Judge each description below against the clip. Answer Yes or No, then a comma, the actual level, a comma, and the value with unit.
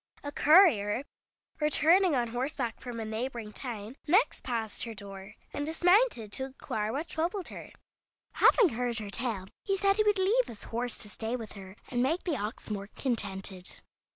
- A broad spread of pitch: Yes, wide, 6.8 semitones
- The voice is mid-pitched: No, high, 245 Hz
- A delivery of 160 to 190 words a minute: Yes, average, 175 wpm